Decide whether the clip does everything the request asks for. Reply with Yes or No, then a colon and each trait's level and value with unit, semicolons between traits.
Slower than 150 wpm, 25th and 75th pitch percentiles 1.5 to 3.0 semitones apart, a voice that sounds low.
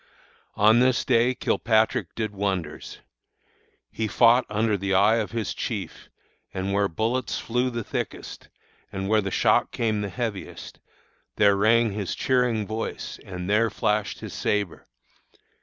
Yes: average, 140 wpm; narrow, 2.5 semitones; low, 110 Hz